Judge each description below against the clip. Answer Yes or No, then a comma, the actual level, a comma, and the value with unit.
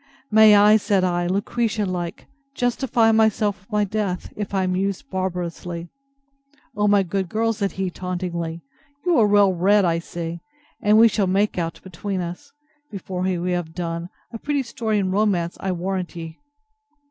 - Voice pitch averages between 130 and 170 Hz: No, high, 190 Hz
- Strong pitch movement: No, average, 3.0 semitones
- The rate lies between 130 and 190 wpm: Yes, average, 170 wpm